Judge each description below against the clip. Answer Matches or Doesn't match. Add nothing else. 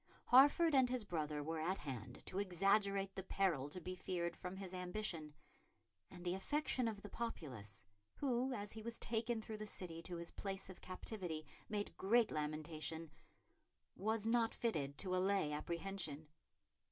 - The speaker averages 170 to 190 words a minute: Doesn't match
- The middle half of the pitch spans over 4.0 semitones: Matches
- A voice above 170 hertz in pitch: Matches